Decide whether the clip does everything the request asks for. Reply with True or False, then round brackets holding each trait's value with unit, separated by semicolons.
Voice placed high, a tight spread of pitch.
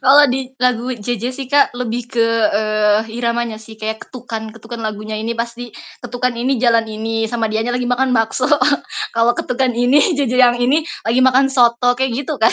True (240 Hz; 2.1 semitones)